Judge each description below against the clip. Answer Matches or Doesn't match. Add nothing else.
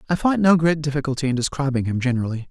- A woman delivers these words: Doesn't match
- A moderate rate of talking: Doesn't match